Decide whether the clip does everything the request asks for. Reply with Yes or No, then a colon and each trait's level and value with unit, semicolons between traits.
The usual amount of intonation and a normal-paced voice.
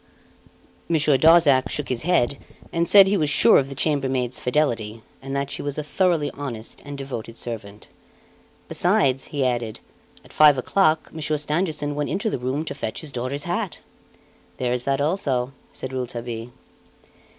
Yes: average, 3.6 semitones; average, 160 wpm